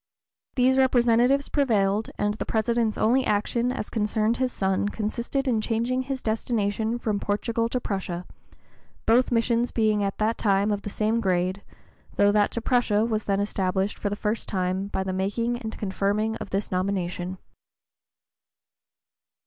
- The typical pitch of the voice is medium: No, high, 215 Hz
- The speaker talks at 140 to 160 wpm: Yes, average, 155 wpm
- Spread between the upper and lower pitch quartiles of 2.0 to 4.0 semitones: Yes, average, 2.8 semitones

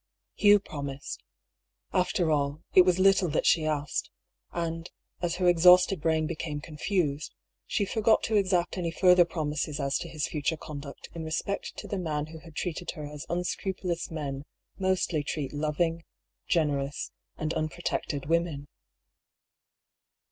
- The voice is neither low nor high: Yes, medium, 165 Hz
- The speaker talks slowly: No, average, 145 wpm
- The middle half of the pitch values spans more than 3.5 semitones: No, average, 3.2 semitones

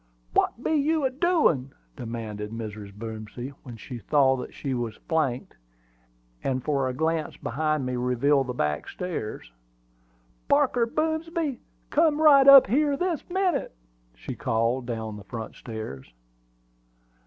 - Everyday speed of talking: No, slow, 130 wpm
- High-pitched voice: No, low, 135 Hz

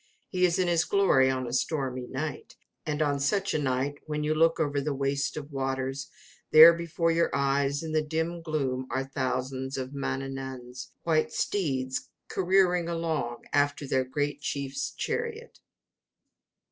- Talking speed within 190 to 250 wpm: No, average, 155 wpm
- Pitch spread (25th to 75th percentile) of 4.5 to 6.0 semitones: No, average, 3.5 semitones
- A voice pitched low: No, medium, 145 Hz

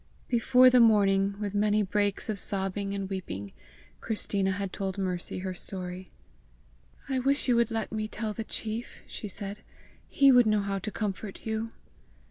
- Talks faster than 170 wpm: No, average, 165 wpm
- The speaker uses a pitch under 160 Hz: No, high, 205 Hz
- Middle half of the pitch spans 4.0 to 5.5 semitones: No, narrow, 2.4 semitones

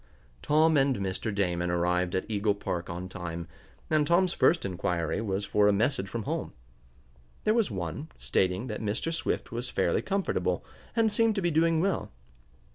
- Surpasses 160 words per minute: Yes, average, 170 wpm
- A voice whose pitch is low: Yes, low, 105 Hz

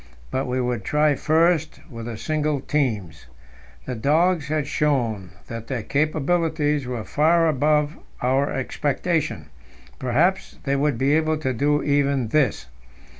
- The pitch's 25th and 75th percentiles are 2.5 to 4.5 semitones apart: Yes, average, 3.5 semitones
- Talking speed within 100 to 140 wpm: Yes, slow, 135 wpm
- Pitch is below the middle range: No, medium, 145 Hz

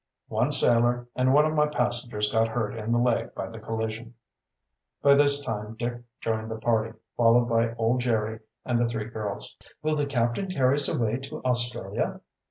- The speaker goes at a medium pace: Yes, average, 180 wpm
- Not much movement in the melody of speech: Yes, narrow, 2.1 semitones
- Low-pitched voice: Yes, low, 120 Hz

